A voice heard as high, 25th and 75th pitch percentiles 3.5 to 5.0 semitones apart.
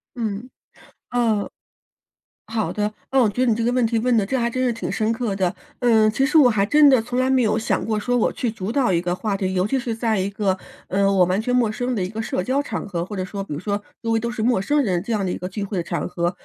Yes: high, 220 Hz; average, 3.8 semitones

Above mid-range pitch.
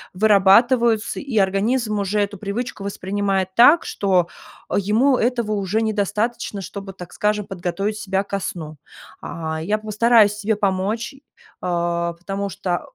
Yes: high, 200 Hz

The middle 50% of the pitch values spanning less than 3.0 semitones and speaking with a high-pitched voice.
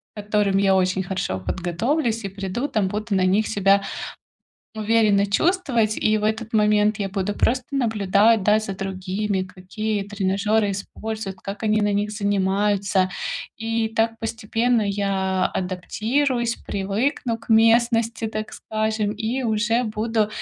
Yes: narrow, 2.4 semitones; high, 210 Hz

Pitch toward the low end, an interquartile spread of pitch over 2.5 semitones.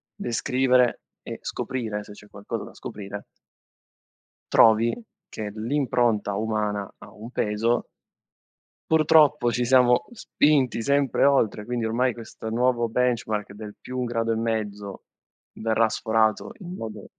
Yes: low, 115 Hz; average, 2.9 semitones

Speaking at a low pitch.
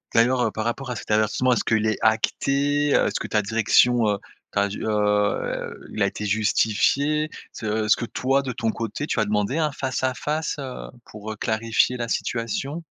Yes: low, 115 Hz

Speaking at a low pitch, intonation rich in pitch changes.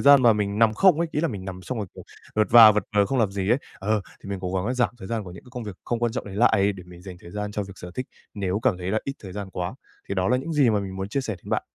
No: low, 105 Hz; average, 3.9 semitones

